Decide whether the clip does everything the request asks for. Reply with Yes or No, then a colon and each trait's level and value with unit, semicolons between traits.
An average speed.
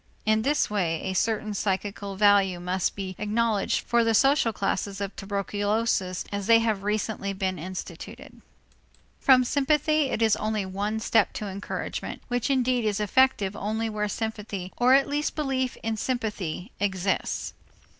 Yes: average, 150 wpm